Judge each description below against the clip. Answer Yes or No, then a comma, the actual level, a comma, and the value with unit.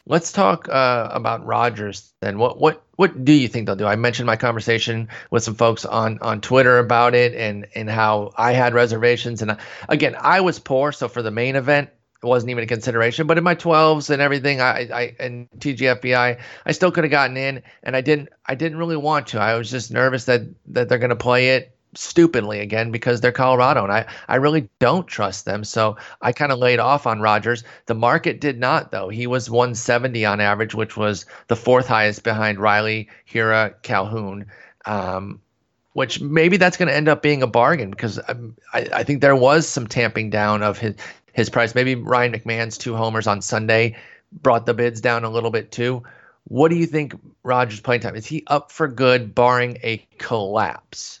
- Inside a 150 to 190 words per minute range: No, fast, 205 wpm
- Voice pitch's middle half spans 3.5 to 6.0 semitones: No, average, 2.9 semitones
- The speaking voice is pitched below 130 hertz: Yes, low, 120 Hz